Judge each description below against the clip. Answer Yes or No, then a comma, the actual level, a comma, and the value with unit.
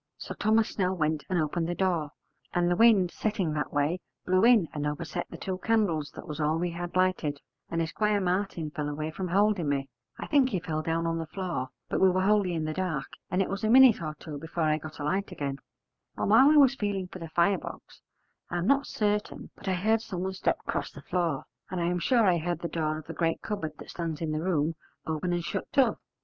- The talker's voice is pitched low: No, medium, 175 Hz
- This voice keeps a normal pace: No, fast, 240 wpm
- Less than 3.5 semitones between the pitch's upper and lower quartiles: No, average, 3.9 semitones